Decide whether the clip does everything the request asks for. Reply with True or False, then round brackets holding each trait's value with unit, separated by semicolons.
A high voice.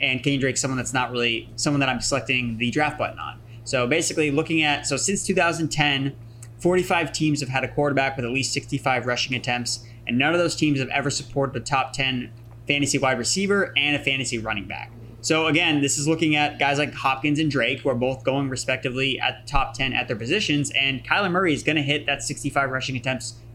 False (135 Hz)